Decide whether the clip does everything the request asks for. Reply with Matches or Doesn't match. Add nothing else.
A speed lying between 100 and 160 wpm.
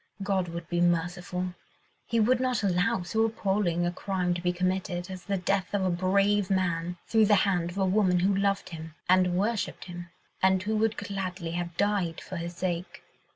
Doesn't match